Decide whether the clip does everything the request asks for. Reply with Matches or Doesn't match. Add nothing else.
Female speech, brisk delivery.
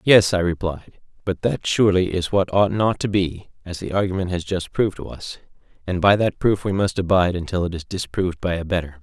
Doesn't match